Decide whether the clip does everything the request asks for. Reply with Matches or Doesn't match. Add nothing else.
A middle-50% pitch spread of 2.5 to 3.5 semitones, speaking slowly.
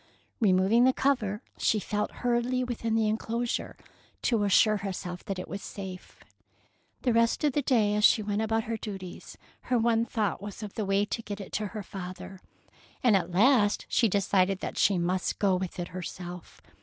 Doesn't match